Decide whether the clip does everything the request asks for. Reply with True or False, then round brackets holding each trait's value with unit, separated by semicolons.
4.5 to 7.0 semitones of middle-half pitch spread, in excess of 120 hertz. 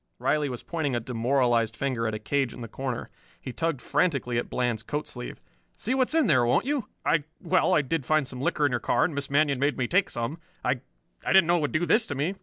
True (5.0 semitones; 140 Hz)